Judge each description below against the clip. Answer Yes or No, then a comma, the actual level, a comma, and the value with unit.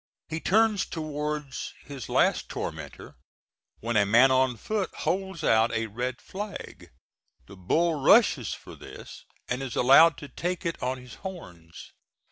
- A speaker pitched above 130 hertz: Yes, medium, 140 Hz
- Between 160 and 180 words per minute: No, average, 145 wpm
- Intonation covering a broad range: Yes, wide, 5.7 semitones